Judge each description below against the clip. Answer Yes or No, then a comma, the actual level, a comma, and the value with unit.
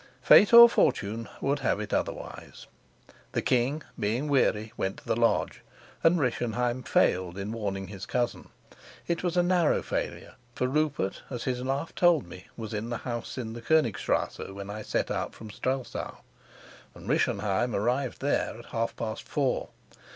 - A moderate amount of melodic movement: Yes, average, 4.6 semitones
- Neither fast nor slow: Yes, average, 165 wpm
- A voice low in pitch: Yes, low, 120 Hz